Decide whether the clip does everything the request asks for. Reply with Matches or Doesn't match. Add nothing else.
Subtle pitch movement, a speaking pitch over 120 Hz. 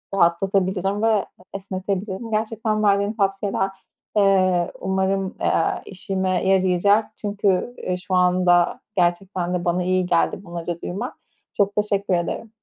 Matches